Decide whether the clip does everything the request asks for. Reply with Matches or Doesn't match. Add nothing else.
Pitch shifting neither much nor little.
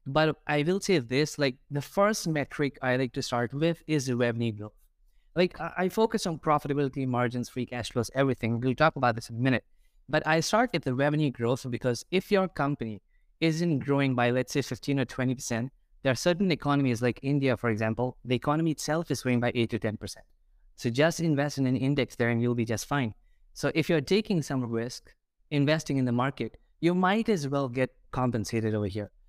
Matches